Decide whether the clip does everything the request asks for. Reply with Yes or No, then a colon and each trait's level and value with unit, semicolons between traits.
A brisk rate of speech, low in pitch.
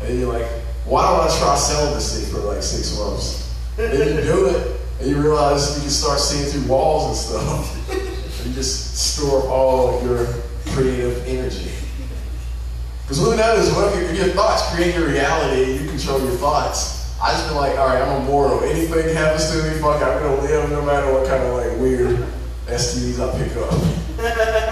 No: average, 190 wpm; low, 130 Hz